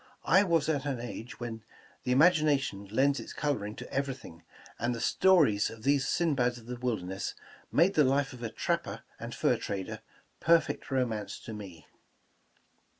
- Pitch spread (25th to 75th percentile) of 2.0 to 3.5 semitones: No, average, 4.5 semitones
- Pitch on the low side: Yes, low, 125 Hz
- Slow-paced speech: No, average, 170 wpm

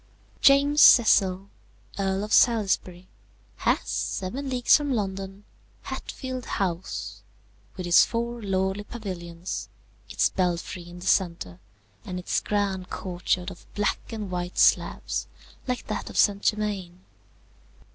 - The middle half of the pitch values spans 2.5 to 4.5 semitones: Yes, average, 3.3 semitones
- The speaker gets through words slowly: Yes, slow, 120 wpm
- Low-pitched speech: No, high, 195 Hz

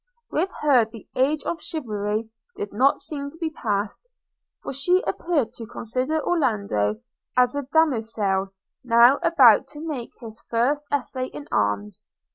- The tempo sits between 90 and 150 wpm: Yes, average, 145 wpm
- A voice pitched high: Yes, very high, 255 Hz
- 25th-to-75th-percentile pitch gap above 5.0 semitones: Yes, wide, 5.4 semitones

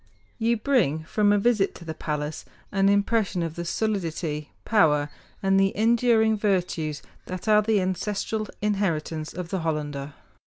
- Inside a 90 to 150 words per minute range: Yes, average, 145 wpm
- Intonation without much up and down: No, average, 5.1 semitones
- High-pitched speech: Yes, high, 195 Hz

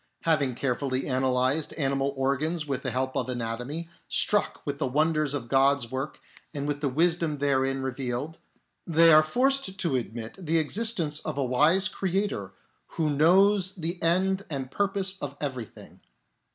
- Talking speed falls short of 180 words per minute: Yes, average, 155 wpm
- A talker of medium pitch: Yes, medium, 145 Hz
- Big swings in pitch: No, average, 4.2 semitones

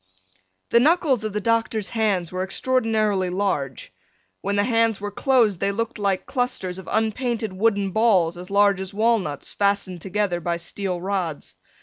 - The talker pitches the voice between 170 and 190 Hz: No, high, 200 Hz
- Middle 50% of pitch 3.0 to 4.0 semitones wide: Yes, average, 3.3 semitones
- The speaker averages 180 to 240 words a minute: No, average, 155 wpm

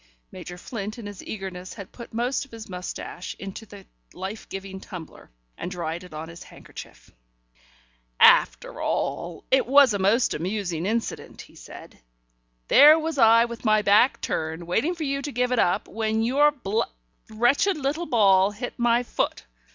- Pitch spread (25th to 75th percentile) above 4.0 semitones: Yes, average, 4.7 semitones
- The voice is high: Yes, high, 215 Hz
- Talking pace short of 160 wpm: No, average, 165 wpm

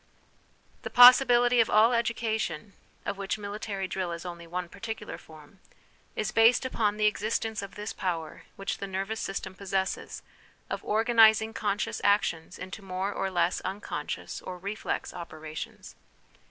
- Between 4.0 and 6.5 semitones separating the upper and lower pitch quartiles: No, average, 3.0 semitones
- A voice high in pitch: Yes, high, 200 Hz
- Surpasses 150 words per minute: No, average, 145 wpm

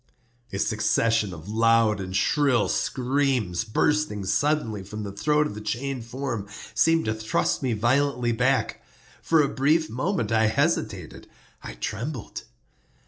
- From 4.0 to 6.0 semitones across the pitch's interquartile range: Yes, average, 4.8 semitones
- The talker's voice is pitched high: No, low, 115 Hz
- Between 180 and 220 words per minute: No, slow, 135 wpm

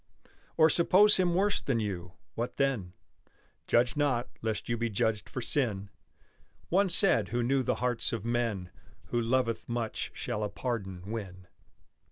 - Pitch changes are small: No, average, 4.2 semitones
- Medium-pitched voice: No, low, 120 Hz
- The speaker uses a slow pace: No, average, 155 wpm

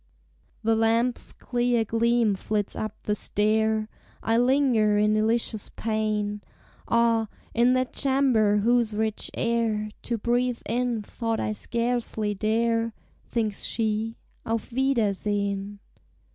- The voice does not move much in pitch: Yes, narrow, 1.8 semitones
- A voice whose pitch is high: Yes, high, 225 Hz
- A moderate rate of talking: No, slow, 115 wpm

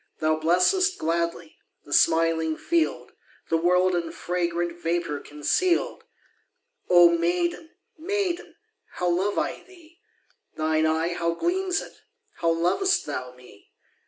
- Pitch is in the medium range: Yes, medium, 170 Hz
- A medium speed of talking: No, slow, 120 wpm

